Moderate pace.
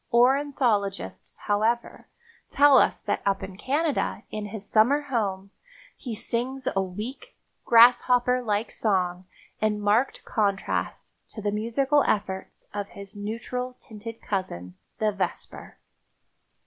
No: slow, 120 wpm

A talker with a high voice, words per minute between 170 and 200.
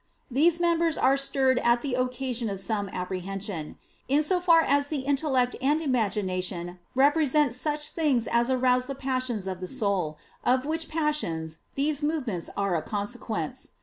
No: very high, 255 Hz; average, 155 wpm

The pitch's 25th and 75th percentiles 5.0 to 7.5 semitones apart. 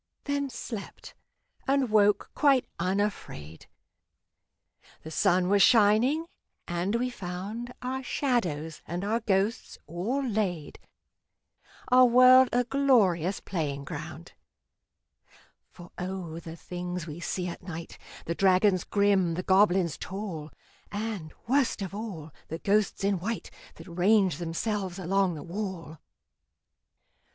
No: average, 4.6 semitones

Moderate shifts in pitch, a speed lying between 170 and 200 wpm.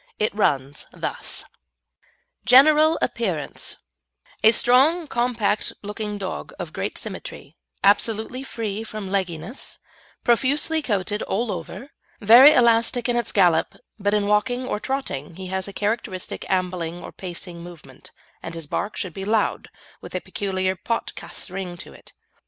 No: average, 4.4 semitones; average, 140 wpm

